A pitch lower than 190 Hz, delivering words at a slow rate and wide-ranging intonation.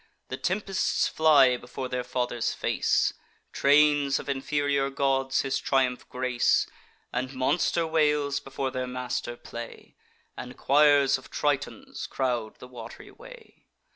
No: low, 135 Hz; slow, 125 wpm; narrow, 2.5 semitones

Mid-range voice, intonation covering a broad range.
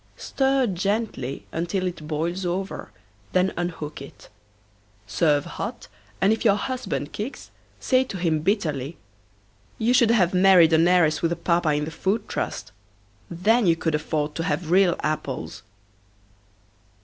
No: medium, 175 Hz; average, 4.1 semitones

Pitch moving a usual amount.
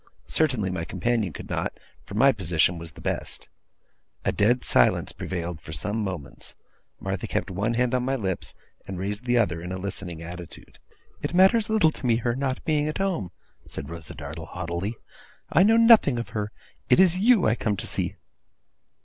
No: wide, 7.4 semitones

